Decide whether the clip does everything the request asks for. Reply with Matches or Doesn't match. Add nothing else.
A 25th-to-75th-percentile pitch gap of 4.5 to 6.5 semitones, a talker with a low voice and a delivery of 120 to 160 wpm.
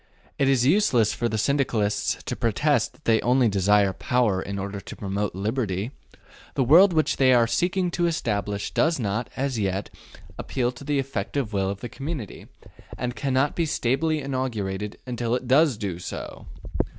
Doesn't match